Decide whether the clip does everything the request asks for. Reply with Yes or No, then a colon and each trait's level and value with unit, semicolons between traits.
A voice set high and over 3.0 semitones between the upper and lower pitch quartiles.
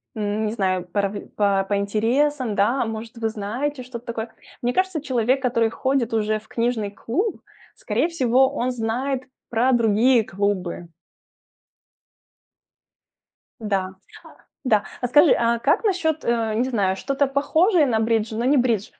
Yes: high, 235 Hz; average, 3.7 semitones